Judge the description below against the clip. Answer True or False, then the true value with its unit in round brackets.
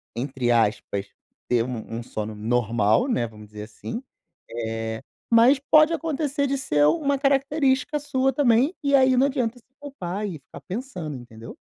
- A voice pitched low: False (225 Hz)